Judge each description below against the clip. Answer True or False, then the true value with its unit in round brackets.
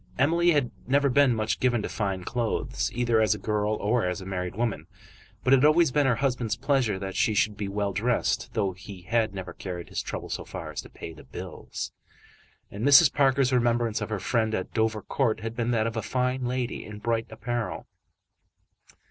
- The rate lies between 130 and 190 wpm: False (205 wpm)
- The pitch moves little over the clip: False (3.5 semitones)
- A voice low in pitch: True (115 Hz)